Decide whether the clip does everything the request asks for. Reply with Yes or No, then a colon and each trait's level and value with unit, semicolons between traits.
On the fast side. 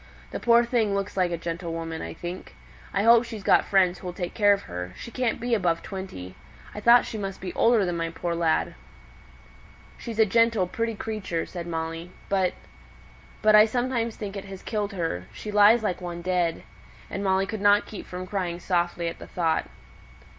No: average, 195 wpm